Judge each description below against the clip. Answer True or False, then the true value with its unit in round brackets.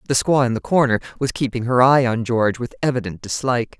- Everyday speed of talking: False (220 wpm)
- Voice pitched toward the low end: True (125 Hz)